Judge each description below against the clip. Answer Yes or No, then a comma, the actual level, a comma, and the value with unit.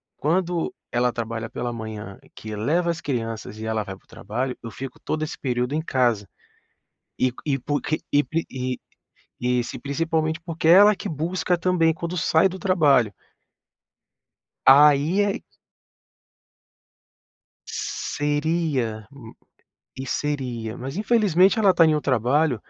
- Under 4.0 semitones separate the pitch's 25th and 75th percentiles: No, average, 5.3 semitones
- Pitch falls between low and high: Yes, medium, 145 Hz